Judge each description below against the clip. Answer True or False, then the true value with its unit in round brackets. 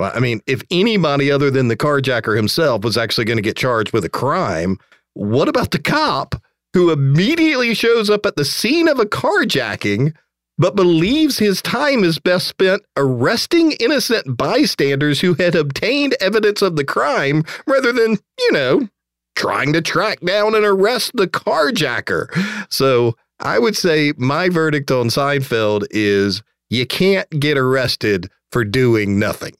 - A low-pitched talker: False (150 Hz)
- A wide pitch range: True (8.8 semitones)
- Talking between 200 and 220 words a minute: False (155 wpm)